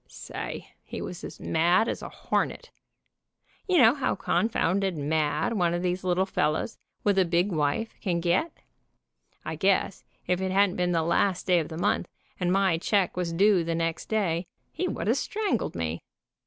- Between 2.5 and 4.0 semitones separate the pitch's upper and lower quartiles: Yes, average, 3.1 semitones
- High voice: No, medium, 180 Hz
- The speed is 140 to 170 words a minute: No, average, 180 wpm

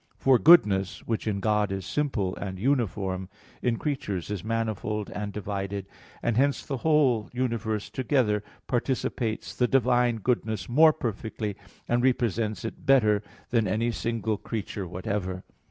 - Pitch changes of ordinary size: Yes, average, 3.5 semitones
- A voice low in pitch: Yes, low, 110 Hz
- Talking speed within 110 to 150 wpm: Yes, average, 140 wpm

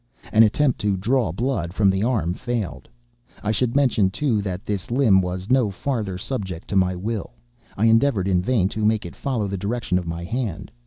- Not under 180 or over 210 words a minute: Yes, average, 200 wpm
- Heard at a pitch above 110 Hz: No, low, 105 Hz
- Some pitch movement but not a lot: Yes, average, 4.5 semitones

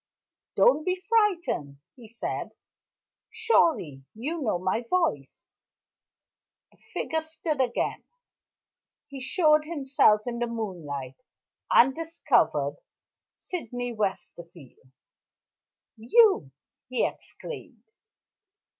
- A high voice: Yes, very high, 250 Hz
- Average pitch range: No, wide, 8.7 semitones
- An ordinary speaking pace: No, slow, 90 wpm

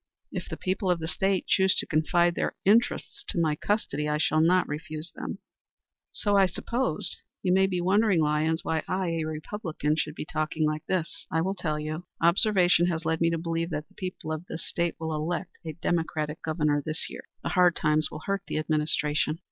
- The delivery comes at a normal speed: No, fast, 210 wpm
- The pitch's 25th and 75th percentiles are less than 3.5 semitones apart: Yes, average, 2.9 semitones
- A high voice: No, medium, 165 Hz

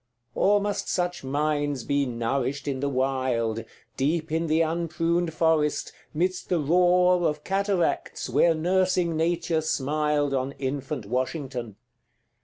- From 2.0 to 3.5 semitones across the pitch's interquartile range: No, average, 4.0 semitones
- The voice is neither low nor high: Yes, medium, 155 Hz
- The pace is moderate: No, slow, 125 wpm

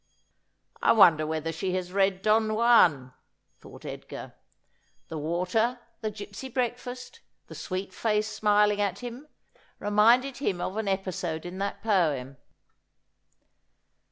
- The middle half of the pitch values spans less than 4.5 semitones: Yes, average, 4.0 semitones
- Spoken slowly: Yes, slow, 130 wpm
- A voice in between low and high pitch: No, high, 200 Hz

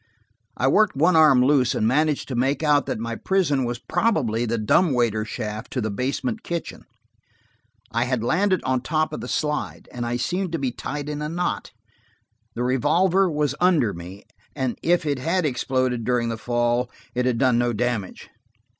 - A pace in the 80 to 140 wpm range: No, average, 185 wpm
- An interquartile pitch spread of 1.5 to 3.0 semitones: No, average, 4.7 semitones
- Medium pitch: No, low, 130 Hz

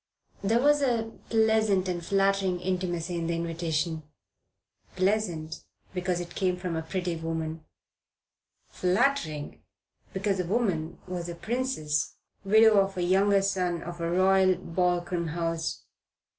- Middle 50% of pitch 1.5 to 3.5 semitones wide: Yes, average, 2.8 semitones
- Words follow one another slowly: Yes, slow, 130 wpm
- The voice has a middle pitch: Yes, medium, 180 Hz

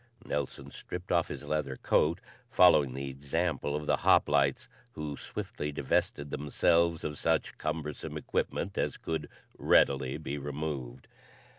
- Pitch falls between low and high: No, very low, 75 Hz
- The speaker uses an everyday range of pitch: No, narrow, 2.2 semitones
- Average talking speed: No, slow, 130 wpm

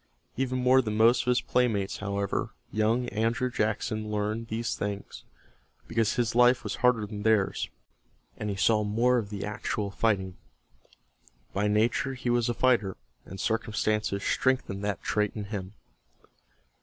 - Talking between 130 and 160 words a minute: Yes, average, 150 wpm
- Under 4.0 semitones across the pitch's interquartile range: Yes, average, 2.8 semitones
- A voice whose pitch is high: No, low, 110 Hz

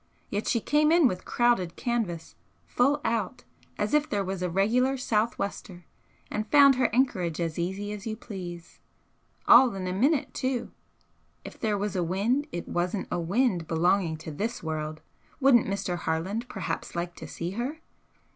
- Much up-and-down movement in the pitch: Yes, wide, 5.8 semitones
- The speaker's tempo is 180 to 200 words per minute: No, average, 165 wpm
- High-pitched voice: Yes, high, 200 Hz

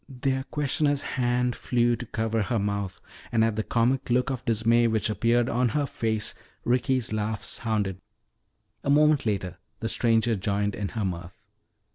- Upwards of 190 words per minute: No, average, 160 wpm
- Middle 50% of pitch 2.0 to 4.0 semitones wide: Yes, average, 2.7 semitones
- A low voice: Yes, low, 115 Hz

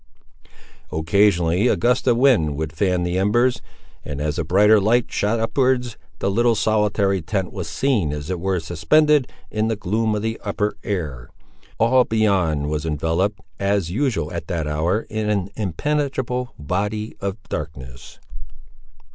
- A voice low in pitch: Yes, low, 100 Hz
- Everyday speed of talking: Yes, average, 150 wpm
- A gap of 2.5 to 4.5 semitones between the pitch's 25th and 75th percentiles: No, wide, 5.5 semitones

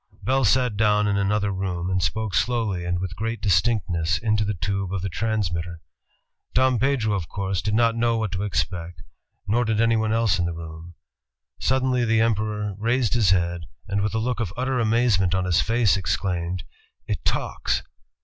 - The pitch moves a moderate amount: Yes, average, 3.9 semitones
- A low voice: Yes, low, 105 Hz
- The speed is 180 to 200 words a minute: Yes, average, 190 wpm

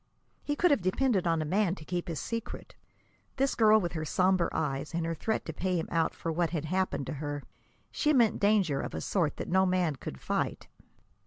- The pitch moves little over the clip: No, average, 4.7 semitones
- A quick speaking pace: Yes, fast, 220 wpm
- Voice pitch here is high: No, medium, 175 Hz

